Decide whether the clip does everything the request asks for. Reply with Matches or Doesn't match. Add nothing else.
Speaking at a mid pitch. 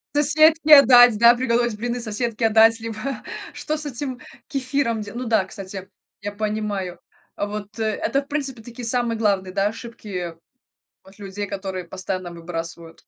Doesn't match